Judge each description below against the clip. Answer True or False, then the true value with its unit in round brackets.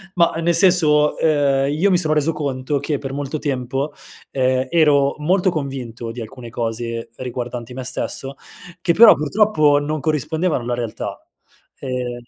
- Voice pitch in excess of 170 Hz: False (140 Hz)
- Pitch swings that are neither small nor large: True (3.6 semitones)